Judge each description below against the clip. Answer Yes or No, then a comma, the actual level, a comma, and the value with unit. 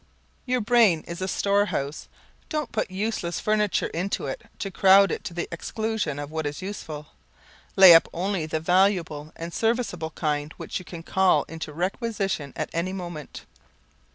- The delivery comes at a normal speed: Yes, average, 160 wpm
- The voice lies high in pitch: No, medium, 180 Hz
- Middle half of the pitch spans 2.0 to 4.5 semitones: Yes, average, 4.0 semitones